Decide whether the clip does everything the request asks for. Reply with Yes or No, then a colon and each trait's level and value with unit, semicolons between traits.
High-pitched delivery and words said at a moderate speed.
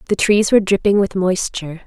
Yes: high, 195 Hz; average, 195 wpm